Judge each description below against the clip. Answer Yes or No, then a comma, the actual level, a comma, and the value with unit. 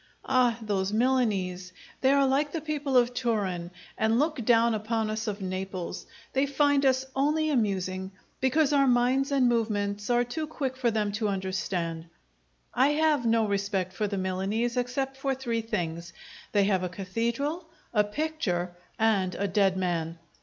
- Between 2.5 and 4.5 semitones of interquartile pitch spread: No, wide, 5.5 semitones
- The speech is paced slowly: No, average, 160 wpm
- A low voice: No, high, 225 Hz